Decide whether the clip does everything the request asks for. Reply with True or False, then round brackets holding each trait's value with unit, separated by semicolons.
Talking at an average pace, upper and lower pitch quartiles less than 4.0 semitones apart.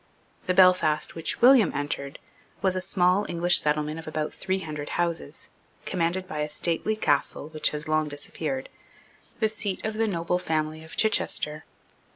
True (160 wpm; 3.5 semitones)